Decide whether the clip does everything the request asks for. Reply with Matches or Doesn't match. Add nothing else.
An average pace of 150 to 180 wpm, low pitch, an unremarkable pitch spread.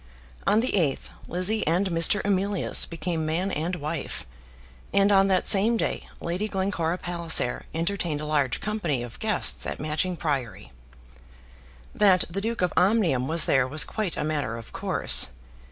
Doesn't match